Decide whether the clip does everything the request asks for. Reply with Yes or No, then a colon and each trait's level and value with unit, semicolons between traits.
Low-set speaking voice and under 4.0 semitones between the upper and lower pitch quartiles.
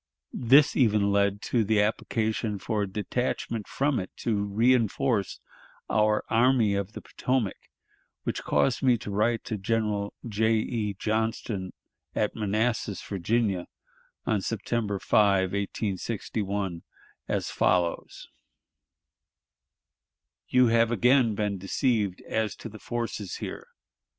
Yes: low, 110 Hz; narrow, 2.5 semitones